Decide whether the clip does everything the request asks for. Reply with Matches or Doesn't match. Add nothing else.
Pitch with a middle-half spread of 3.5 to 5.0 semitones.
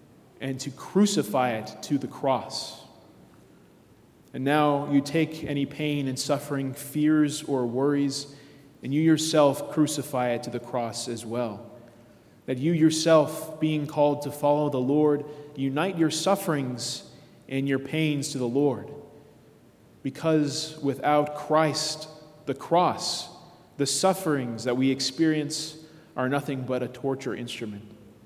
Doesn't match